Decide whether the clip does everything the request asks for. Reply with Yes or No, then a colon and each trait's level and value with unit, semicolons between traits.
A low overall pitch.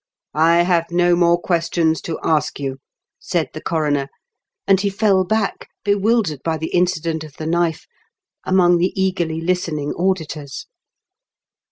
No: medium, 170 Hz